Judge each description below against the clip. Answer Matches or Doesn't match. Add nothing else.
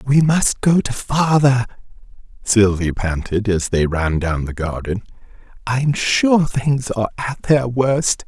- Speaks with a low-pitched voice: Matches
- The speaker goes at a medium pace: Matches